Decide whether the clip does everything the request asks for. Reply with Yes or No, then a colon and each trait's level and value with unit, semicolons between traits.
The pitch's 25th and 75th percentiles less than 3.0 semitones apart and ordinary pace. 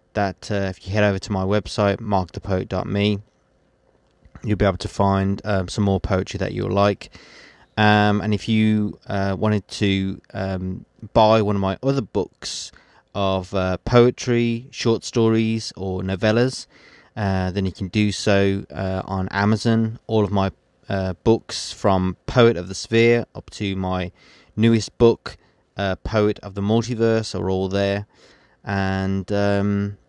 Yes: narrow, 2.4 semitones; average, 155 wpm